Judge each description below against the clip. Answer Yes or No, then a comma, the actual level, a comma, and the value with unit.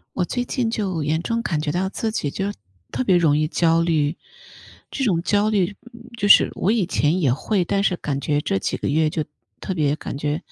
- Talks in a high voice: No, medium, 175 Hz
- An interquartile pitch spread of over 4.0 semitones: Yes, average, 5.1 semitones